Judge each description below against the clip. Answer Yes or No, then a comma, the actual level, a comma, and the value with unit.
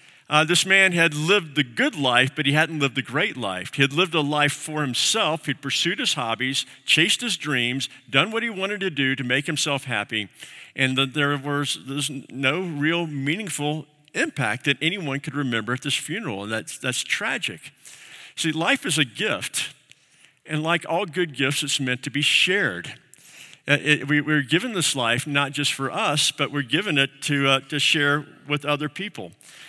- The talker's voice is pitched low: No, medium, 145 Hz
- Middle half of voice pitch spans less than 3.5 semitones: Yes, narrow, 2.5 semitones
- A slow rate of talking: No, average, 195 wpm